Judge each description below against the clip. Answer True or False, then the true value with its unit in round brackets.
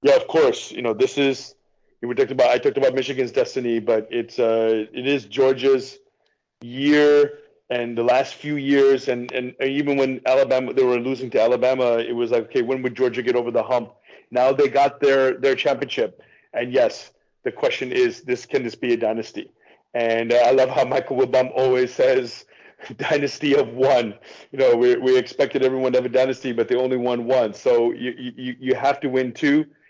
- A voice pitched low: True (130 Hz)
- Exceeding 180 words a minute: True (200 wpm)